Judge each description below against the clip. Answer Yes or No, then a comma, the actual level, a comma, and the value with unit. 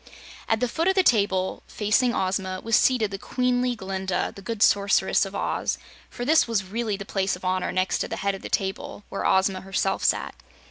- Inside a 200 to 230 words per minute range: Yes, fast, 205 wpm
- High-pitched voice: Yes, high, 200 Hz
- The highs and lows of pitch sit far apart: No, average, 3.5 semitones